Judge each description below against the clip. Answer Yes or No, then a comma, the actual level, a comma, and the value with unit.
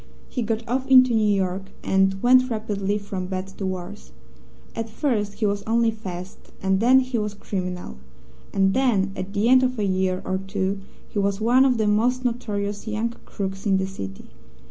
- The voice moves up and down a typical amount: Yes, average, 3.4 semitones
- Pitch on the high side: Yes, high, 205 Hz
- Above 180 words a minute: Yes, average, 190 wpm